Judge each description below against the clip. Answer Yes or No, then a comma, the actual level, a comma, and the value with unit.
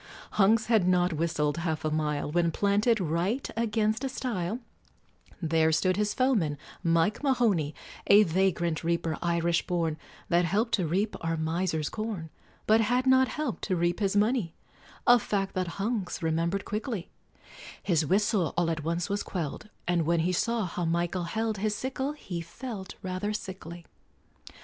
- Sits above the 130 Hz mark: Yes, medium, 185 Hz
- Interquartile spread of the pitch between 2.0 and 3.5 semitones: No, average, 4.3 semitones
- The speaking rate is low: No, average, 160 wpm